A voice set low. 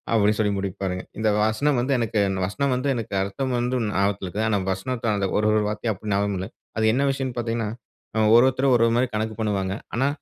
Yes: low, 110 Hz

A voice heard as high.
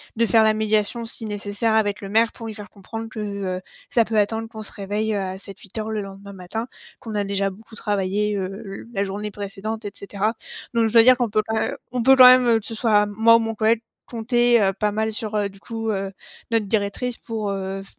Yes: high, 215 Hz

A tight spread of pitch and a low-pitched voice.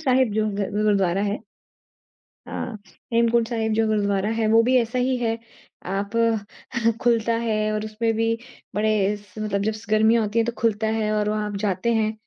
No: narrow, 1.6 semitones; high, 215 Hz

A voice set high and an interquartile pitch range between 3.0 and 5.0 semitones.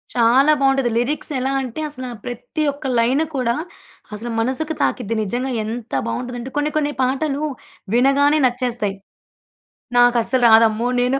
No: very high, 250 Hz; narrow, 2.5 semitones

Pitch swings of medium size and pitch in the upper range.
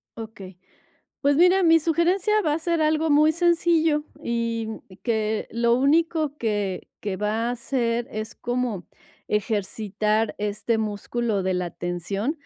No: wide, 6.7 semitones; high, 235 Hz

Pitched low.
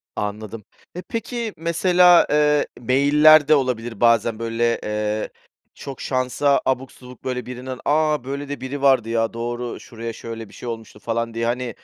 Yes: low, 125 Hz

